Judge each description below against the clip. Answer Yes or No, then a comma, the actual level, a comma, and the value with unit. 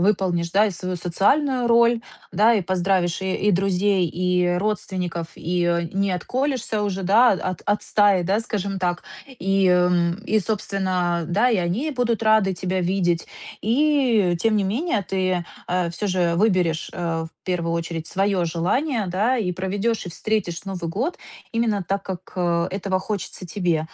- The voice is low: No, high, 190 Hz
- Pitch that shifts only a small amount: No, average, 3.3 semitones